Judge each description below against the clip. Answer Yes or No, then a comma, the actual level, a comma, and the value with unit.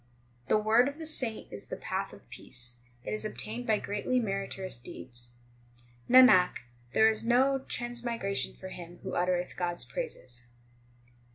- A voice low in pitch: No, high, 215 Hz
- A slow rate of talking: No, average, 160 wpm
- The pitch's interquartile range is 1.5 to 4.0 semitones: No, wide, 5.5 semitones